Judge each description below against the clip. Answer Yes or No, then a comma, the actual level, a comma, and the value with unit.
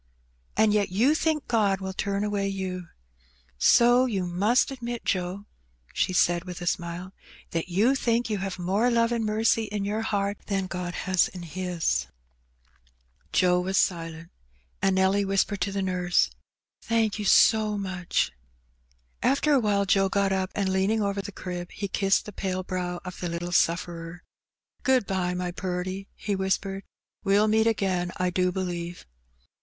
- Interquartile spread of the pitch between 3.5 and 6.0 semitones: No, average, 2.7 semitones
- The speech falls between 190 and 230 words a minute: No, average, 170 wpm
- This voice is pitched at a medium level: No, high, 195 Hz